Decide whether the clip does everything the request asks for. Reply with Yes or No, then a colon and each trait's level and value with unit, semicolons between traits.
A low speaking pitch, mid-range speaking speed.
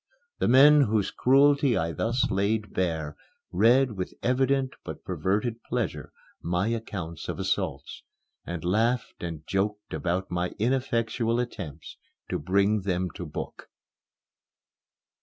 No: low, 105 Hz; slow, 120 wpm